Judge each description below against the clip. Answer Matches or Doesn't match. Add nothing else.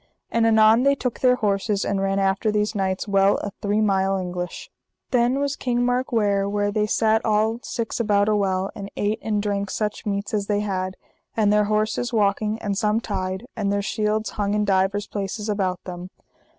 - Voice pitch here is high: Matches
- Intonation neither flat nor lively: Doesn't match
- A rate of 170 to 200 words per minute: Matches